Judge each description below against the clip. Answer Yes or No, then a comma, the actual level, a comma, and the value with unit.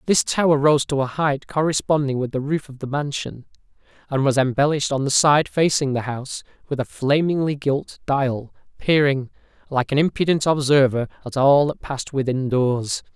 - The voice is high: No, medium, 140 Hz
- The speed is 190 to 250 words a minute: No, average, 175 wpm